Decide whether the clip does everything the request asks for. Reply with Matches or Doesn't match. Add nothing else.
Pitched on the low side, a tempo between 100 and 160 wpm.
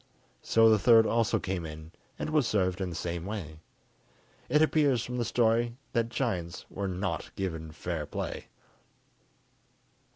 Matches